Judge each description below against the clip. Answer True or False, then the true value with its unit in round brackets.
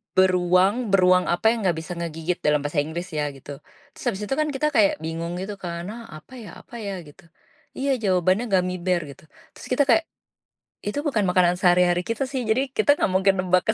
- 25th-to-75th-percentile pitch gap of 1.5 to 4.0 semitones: False (4.6 semitones)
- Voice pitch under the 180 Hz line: False (185 Hz)